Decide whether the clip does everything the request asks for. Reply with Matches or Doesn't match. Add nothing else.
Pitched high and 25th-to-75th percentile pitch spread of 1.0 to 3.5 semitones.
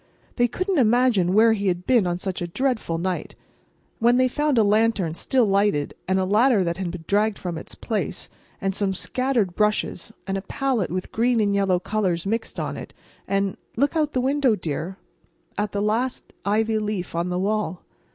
Doesn't match